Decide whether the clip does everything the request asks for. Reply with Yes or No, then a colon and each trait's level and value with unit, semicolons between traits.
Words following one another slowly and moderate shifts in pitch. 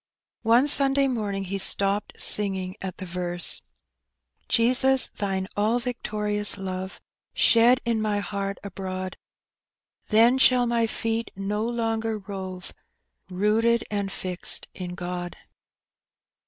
Yes: slow, 120 wpm; average, 3.4 semitones